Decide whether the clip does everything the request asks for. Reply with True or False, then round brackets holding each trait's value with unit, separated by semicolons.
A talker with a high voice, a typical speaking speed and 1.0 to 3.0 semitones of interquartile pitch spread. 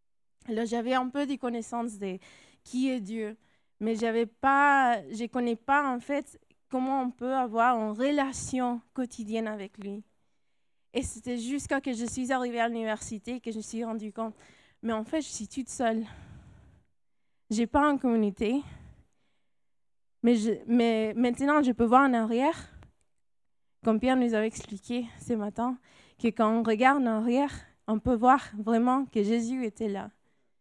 True (235 Hz; 170 wpm; 2.5 semitones)